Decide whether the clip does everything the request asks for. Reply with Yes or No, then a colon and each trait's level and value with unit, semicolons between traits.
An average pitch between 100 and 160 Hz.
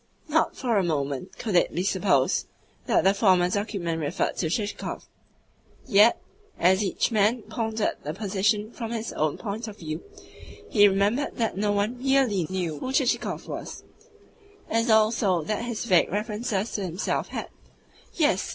No: high, 205 Hz